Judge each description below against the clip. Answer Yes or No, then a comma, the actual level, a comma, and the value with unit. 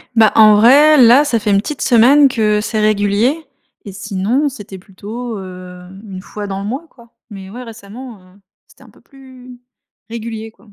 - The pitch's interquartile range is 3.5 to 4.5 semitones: Yes, average, 3.8 semitones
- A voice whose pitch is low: No, high, 220 Hz